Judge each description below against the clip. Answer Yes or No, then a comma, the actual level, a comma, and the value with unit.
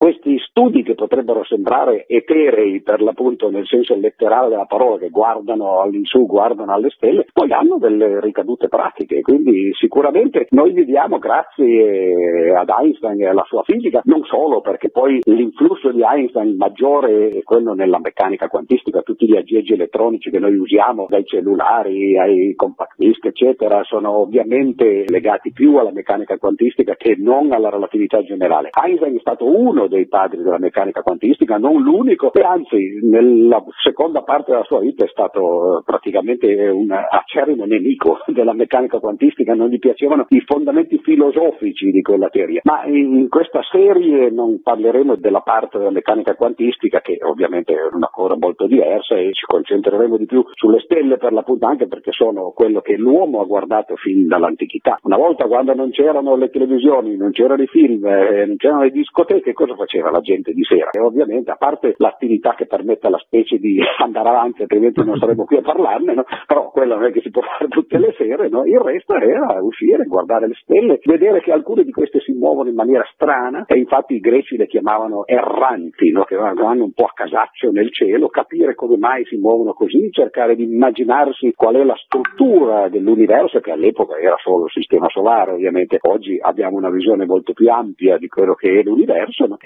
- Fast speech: Yes, fast, 180 wpm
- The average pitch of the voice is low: No, very high, 335 Hz